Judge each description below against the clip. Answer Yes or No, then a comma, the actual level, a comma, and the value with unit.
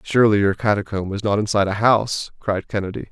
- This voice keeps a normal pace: Yes, average, 190 wpm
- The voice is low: Yes, low, 105 Hz